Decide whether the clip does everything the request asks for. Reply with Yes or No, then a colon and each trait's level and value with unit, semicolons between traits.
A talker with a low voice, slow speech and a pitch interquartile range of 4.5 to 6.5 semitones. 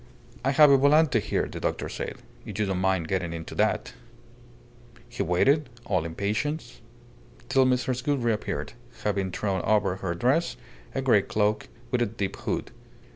No: low, 110 Hz; average, 165 wpm; wide, 5.5 semitones